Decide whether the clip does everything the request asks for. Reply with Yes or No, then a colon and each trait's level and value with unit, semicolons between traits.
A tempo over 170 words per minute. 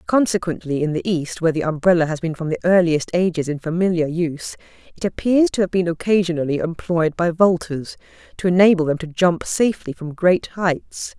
Yes: average, 180 wpm